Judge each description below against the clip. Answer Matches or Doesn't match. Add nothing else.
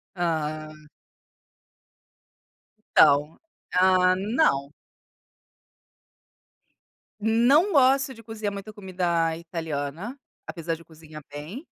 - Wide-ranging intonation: Matches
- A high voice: Doesn't match